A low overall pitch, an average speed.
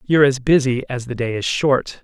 No: low, 130 Hz; fast, 235 wpm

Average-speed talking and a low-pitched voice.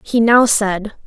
No: average, 170 wpm; high, 220 Hz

